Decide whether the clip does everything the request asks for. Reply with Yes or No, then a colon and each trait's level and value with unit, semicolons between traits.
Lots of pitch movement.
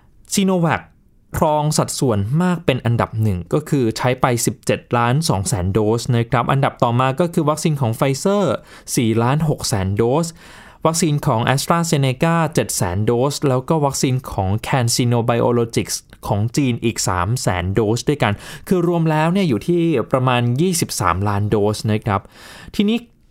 Yes: wide, 5.7 semitones